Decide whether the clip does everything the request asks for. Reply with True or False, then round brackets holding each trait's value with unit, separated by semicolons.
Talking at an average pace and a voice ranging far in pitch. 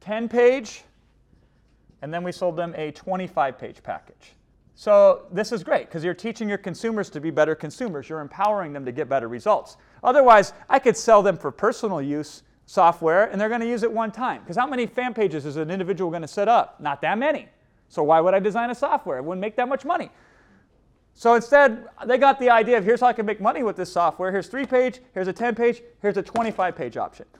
False (220 wpm; 5.7 semitones)